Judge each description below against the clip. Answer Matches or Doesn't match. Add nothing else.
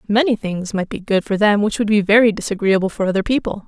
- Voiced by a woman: Matches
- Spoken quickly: Matches